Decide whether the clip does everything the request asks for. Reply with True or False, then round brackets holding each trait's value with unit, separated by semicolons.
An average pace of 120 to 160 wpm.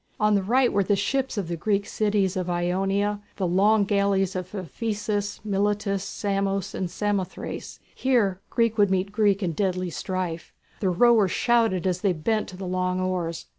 False (170 wpm)